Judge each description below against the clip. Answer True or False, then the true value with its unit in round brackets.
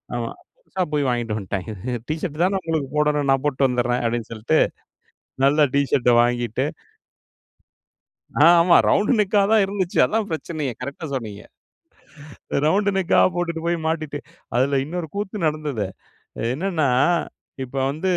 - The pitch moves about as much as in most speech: False (5.8 semitones)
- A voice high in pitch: False (150 Hz)